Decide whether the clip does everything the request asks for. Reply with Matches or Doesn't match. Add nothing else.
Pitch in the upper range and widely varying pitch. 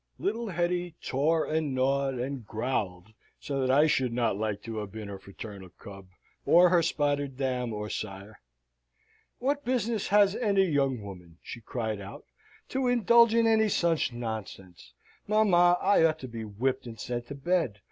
Doesn't match